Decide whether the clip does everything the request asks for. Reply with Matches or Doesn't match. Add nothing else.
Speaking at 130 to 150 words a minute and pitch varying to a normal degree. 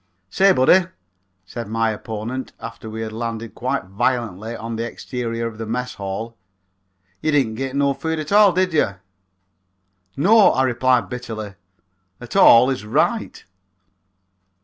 Matches